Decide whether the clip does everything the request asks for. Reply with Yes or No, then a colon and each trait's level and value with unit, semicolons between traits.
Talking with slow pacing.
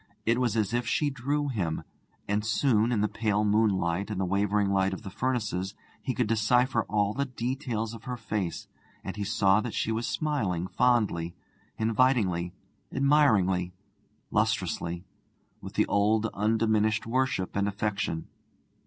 No: average, 150 wpm